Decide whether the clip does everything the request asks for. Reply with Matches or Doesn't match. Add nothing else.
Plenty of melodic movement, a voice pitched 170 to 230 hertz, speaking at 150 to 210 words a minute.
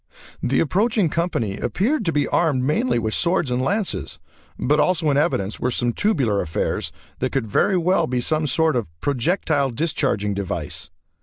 Doesn't match